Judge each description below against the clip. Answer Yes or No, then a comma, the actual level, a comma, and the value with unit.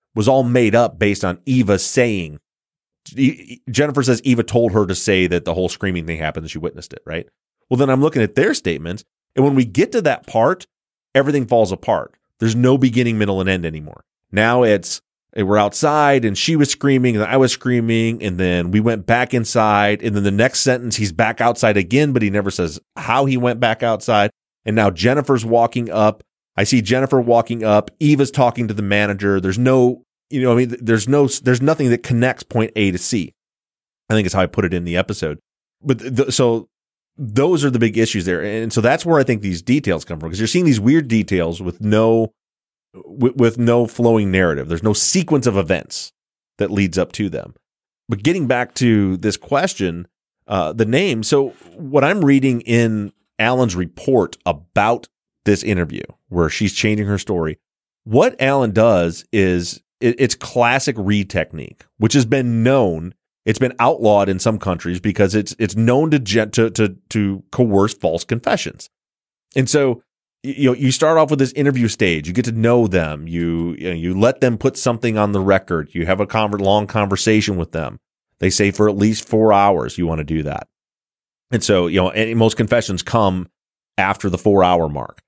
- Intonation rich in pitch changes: No, average, 4.4 semitones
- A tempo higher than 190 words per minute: Yes, average, 200 wpm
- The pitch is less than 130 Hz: Yes, low, 110 Hz